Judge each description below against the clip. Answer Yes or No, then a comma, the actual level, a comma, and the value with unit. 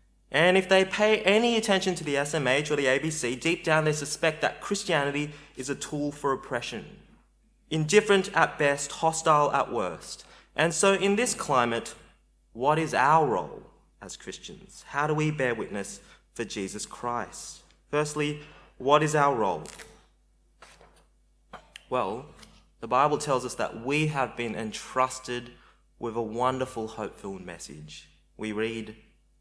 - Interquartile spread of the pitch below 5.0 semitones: No, average, 5.3 semitones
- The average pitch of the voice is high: No, medium, 140 Hz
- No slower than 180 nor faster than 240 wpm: No, average, 145 wpm